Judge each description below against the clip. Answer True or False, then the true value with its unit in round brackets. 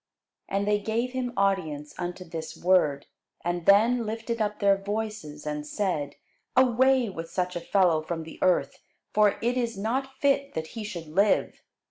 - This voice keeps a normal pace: True (165 wpm)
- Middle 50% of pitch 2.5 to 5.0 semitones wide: False (5.6 semitones)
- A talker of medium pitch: False (200 Hz)